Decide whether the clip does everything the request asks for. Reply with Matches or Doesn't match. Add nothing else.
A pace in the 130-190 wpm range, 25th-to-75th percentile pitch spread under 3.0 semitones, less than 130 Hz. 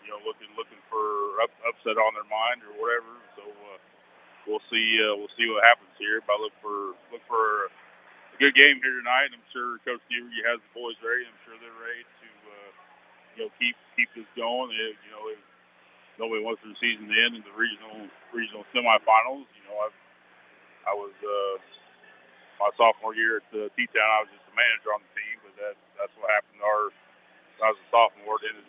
Doesn't match